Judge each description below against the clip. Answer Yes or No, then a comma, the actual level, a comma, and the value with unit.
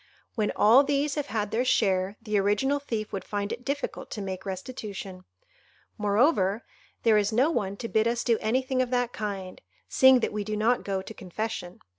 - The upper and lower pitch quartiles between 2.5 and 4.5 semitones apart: Yes, average, 3.7 semitones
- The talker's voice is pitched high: Yes, high, 215 Hz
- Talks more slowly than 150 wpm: No, average, 190 wpm